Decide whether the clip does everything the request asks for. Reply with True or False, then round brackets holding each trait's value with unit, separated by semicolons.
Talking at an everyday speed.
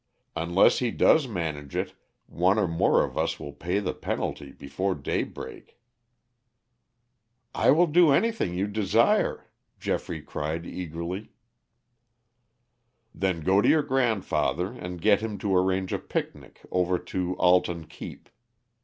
False (130 wpm)